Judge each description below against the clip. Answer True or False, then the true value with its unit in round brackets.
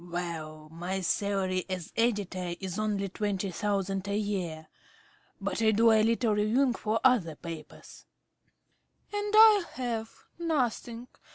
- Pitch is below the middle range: False (205 Hz)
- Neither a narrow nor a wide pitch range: True (3.9 semitones)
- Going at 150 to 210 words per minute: False (140 wpm)